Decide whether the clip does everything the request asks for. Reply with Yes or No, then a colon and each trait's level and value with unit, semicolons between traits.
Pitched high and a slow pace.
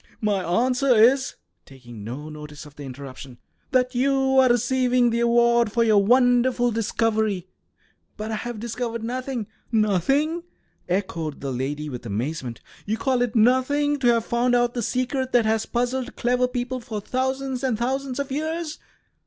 No: high, 240 Hz; average, 160 wpm